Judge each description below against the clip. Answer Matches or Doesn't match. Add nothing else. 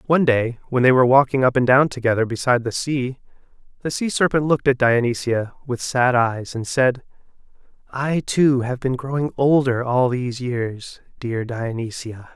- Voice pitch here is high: Doesn't match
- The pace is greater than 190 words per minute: Doesn't match